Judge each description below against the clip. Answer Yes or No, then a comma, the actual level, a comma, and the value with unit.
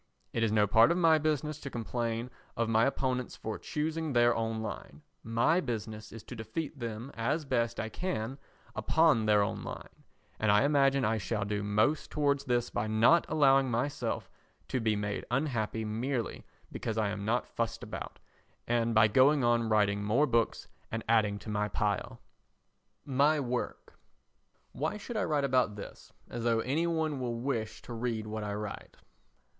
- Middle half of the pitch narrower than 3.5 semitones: No, average, 4.2 semitones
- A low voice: Yes, low, 115 Hz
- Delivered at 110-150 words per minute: No, average, 175 wpm